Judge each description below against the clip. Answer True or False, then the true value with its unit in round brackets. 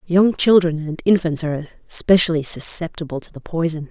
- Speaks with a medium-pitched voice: True (165 Hz)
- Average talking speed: True (155 wpm)